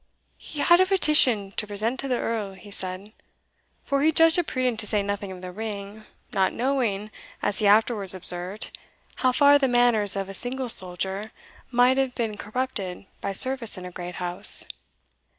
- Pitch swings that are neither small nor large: Yes, average, 4.7 semitones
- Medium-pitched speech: No, high, 215 Hz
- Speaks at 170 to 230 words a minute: Yes, average, 180 wpm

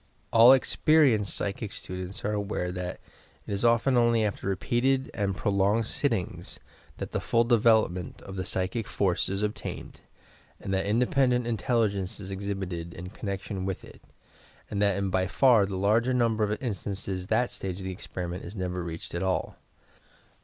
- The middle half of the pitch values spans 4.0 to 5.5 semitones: No, average, 3.6 semitones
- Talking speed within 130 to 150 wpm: No, average, 165 wpm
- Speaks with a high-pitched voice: No, low, 100 Hz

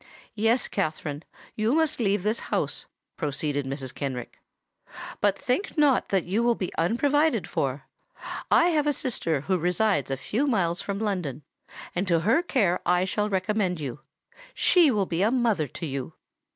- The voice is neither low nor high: No, high, 195 Hz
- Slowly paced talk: No, average, 165 wpm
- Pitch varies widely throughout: Yes, wide, 6.6 semitones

